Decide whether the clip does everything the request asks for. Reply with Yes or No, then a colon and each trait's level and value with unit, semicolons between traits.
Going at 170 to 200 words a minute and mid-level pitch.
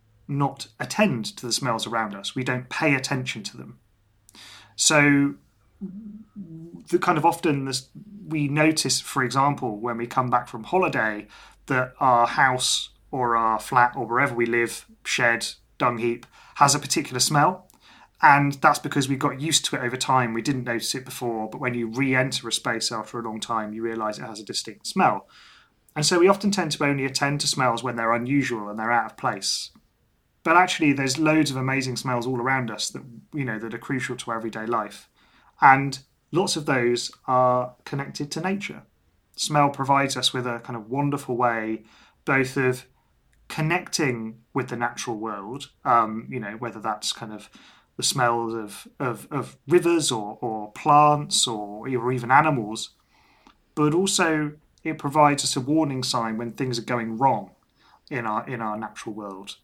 No: average, 180 wpm; low, 130 Hz